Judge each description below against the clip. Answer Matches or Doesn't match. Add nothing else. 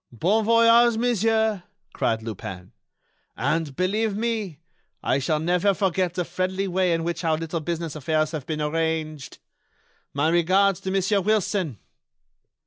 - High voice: Doesn't match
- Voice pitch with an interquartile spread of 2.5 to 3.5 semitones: Doesn't match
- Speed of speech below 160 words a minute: Matches